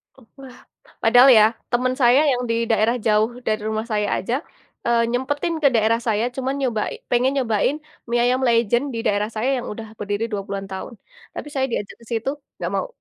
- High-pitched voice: Yes, high, 230 Hz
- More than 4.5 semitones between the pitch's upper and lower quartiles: No, average, 2.9 semitones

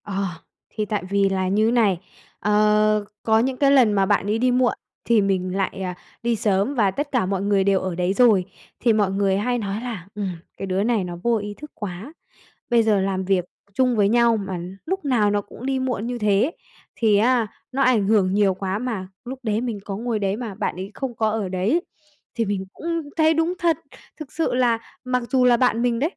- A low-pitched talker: No, high, 215 Hz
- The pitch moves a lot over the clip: No, average, 4.0 semitones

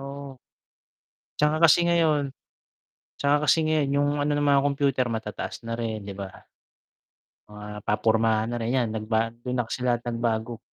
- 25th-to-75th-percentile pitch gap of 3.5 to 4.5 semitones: Yes, average, 4.2 semitones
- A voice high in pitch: No, low, 120 Hz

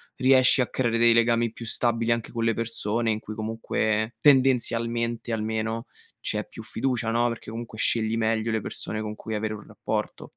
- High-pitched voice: No, low, 115 Hz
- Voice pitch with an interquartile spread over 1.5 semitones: No, narrow, 1.1 semitones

